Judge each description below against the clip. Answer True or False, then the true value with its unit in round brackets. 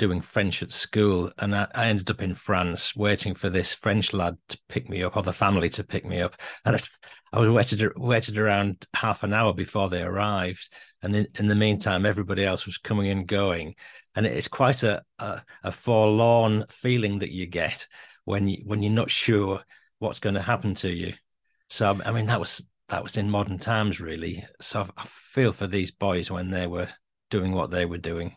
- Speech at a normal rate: False (210 wpm)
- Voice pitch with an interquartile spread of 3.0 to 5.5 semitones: False (2.6 semitones)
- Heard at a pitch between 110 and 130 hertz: False (100 Hz)